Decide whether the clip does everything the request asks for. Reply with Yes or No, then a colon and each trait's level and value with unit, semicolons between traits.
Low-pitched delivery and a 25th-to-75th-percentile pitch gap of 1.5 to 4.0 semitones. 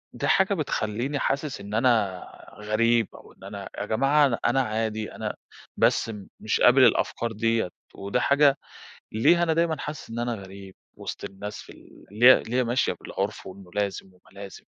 No: low, 115 Hz; average, 4.7 semitones